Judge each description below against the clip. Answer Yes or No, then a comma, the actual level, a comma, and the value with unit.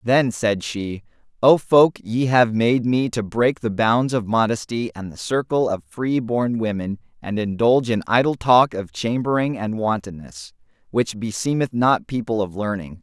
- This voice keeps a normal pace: Yes, average, 170 wpm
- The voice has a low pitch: Yes, low, 115 Hz